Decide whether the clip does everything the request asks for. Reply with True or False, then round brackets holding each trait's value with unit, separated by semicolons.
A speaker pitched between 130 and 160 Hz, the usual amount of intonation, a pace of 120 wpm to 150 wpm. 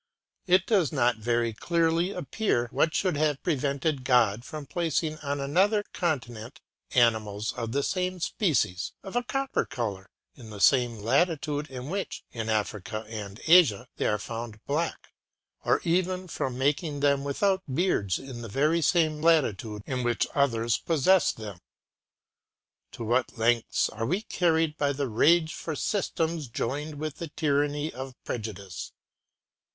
False (140 Hz; 6.0 semitones; 145 wpm)